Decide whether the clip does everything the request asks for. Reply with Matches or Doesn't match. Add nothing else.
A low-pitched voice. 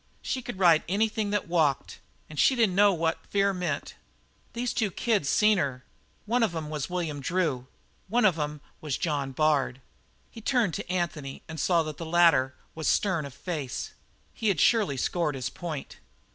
Doesn't match